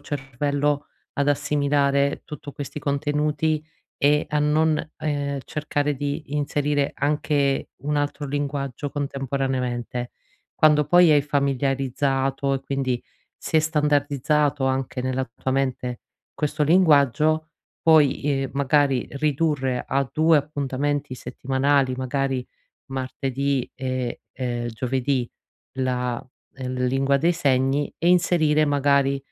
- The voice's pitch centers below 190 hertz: Yes, medium, 140 Hz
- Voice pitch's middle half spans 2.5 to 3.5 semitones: No, narrow, 1.9 semitones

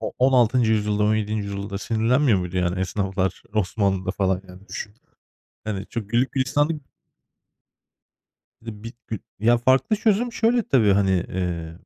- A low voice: Yes, low, 105 Hz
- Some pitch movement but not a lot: Yes, average, 4.4 semitones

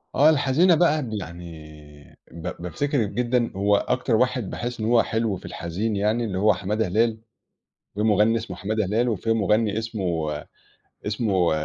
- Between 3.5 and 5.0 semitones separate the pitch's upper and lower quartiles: Yes, average, 4.1 semitones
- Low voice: Yes, low, 110 Hz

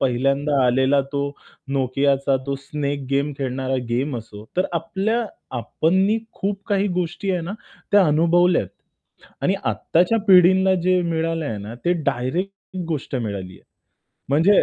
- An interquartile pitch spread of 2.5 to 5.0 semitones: No, wide, 5.4 semitones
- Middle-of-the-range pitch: Yes, medium, 150 Hz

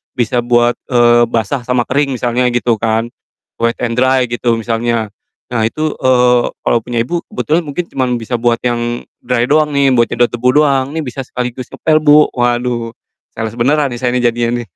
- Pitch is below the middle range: Yes, low, 120 Hz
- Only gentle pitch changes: Yes, narrow, 2.0 semitones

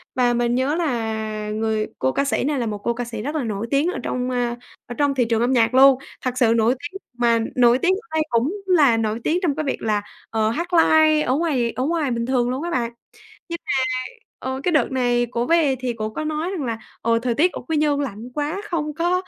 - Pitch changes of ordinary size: Yes, average, 4.6 semitones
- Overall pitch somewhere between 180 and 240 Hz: No, very high, 255 Hz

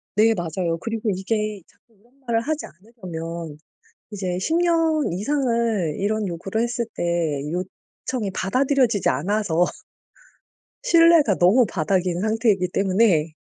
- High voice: Yes, high, 205 Hz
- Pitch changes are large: No, average, 4.9 semitones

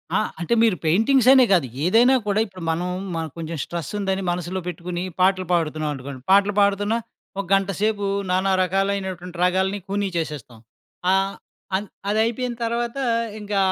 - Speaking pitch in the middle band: No, high, 195 Hz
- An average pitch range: Yes, average, 3.0 semitones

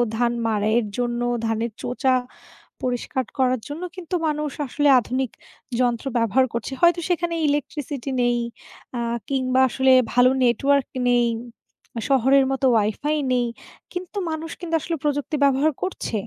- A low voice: No, very high, 260 Hz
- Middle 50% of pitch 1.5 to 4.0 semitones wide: Yes, average, 3.5 semitones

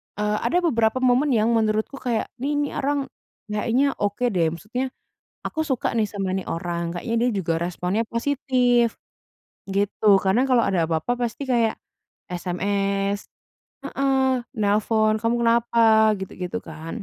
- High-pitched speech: Yes, high, 220 Hz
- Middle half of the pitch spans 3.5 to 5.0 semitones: Yes, average, 4.1 semitones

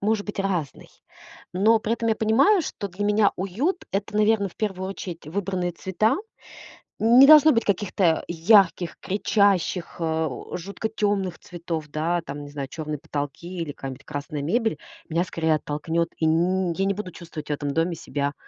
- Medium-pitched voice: Yes, medium, 180 Hz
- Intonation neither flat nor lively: Yes, average, 4.4 semitones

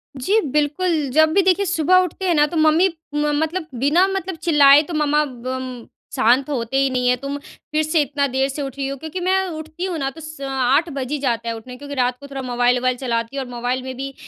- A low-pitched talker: No, very high, 285 Hz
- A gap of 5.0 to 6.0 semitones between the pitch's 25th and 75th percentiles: No, average, 3.5 semitones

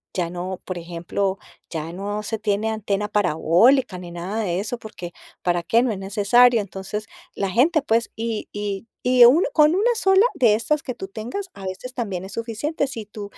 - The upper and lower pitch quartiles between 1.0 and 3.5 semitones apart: No, average, 4.2 semitones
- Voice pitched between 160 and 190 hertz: No, high, 210 Hz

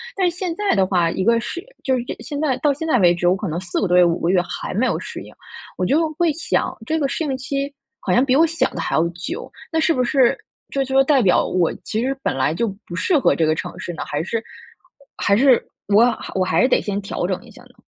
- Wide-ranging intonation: Yes, wide, 7.8 semitones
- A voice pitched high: Yes, high, 235 Hz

